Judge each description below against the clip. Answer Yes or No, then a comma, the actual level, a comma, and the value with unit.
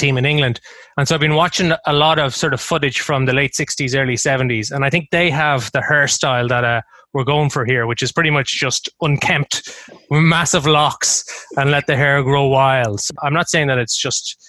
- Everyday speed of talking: No, fast, 225 wpm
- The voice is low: No, medium, 145 Hz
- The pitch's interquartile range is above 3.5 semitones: No, average, 2.9 semitones